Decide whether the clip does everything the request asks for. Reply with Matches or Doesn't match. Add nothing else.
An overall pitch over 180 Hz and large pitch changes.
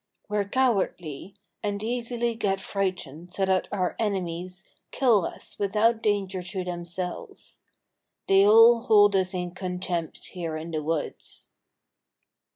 Doesn't match